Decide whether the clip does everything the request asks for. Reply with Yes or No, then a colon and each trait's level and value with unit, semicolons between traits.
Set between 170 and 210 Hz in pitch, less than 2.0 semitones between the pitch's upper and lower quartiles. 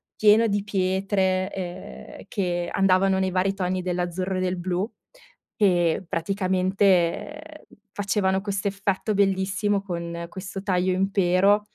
Yes: high, 190 Hz; narrow, 1.5 semitones